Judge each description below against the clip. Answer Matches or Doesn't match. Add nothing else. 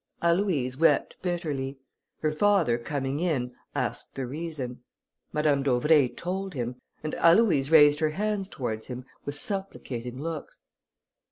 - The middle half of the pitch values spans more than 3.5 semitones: Matches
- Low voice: Doesn't match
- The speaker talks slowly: Matches